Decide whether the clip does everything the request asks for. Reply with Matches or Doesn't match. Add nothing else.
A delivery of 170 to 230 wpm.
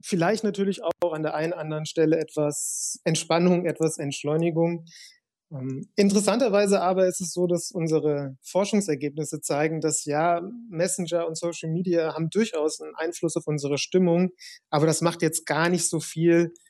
Doesn't match